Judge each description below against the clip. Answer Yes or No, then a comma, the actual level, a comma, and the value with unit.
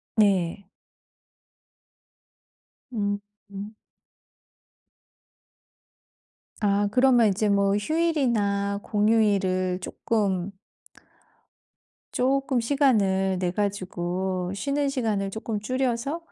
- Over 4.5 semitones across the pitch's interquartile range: No, average, 3.7 semitones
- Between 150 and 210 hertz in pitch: Yes, high, 205 Hz